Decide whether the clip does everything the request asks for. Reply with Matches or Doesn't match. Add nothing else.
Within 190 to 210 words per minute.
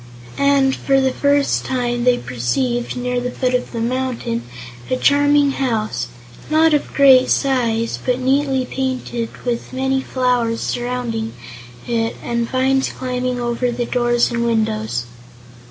Doesn't match